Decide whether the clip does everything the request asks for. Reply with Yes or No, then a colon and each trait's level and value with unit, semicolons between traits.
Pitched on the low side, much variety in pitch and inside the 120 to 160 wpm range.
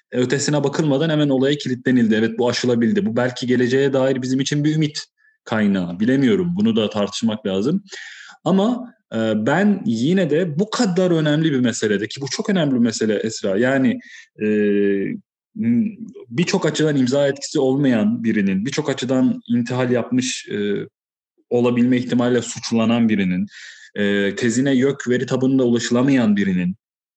Yes: low, 130 Hz; wide, 6.3 semitones; average, 125 wpm